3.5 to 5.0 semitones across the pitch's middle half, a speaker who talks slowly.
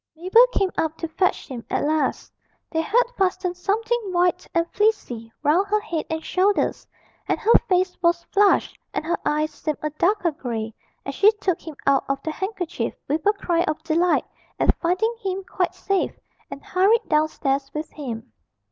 No: average, 4.2 semitones; average, 175 wpm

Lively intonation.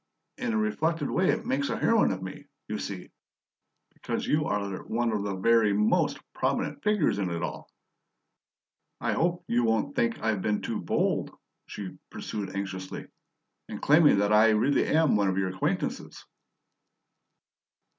Yes: wide, 8.2 semitones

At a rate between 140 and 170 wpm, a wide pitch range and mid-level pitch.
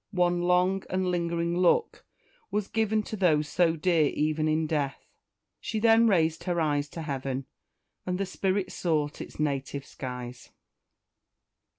No: average, 145 wpm; average, 3.8 semitones; medium, 170 Hz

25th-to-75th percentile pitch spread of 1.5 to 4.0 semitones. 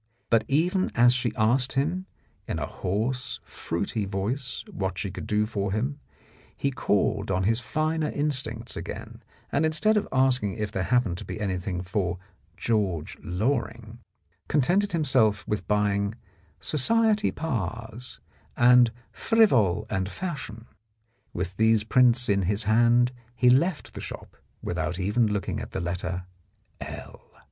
No: average, 5.0 semitones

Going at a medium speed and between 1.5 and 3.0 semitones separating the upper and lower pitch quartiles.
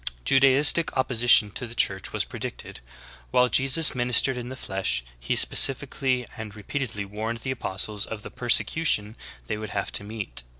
No: average, 170 wpm; average, 3.9 semitones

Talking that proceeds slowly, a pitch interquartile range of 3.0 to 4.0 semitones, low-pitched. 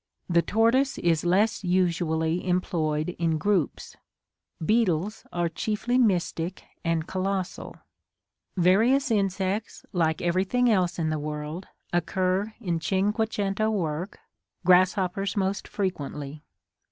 No: slow, 105 wpm; average, 3.5 semitones; medium, 185 Hz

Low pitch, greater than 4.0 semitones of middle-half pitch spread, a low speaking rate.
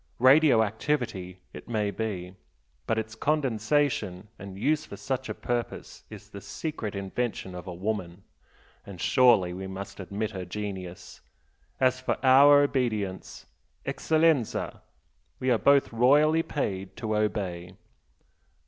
Yes: low, 110 Hz; wide, 5.4 semitones; slow, 130 wpm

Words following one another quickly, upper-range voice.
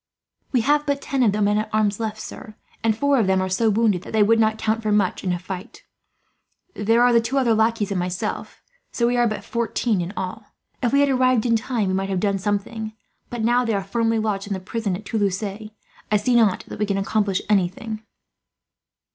Yes: fast, 230 wpm; high, 215 Hz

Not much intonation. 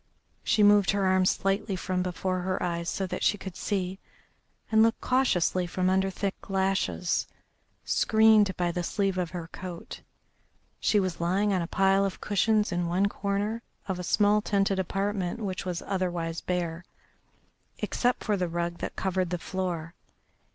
Yes: narrow, 2.2 semitones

